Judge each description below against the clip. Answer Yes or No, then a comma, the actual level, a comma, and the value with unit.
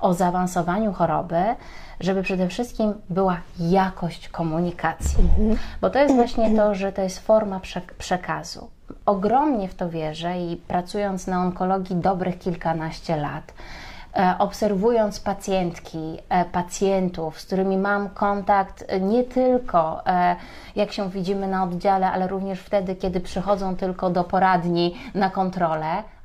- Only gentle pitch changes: Yes, narrow, 2.3 semitones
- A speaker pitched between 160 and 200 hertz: Yes, high, 190 Hz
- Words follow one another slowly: No, average, 125 wpm